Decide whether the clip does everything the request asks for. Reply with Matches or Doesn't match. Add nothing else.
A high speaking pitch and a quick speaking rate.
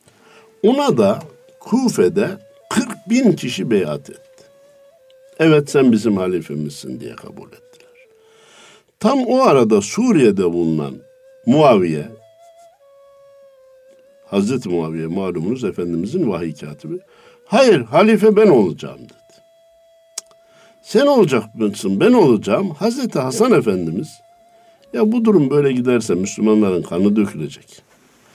Doesn't match